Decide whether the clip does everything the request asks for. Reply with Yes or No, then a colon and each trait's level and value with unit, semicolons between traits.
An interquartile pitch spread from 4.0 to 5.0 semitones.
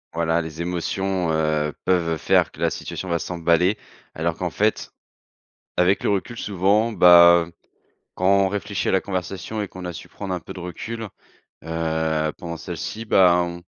No: average, 2.7 semitones